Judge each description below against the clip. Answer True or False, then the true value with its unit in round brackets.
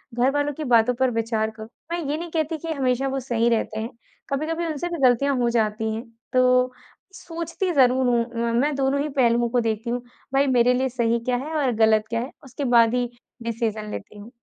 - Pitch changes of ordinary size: True (3.3 semitones)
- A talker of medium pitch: False (250 Hz)